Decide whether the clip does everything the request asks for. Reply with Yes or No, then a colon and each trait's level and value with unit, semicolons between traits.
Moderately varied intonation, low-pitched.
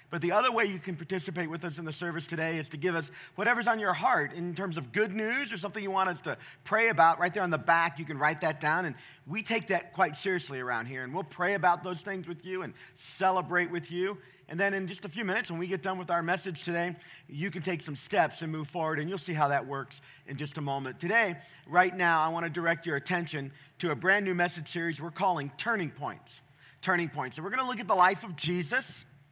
No: average, 3.5 semitones; medium, 175 Hz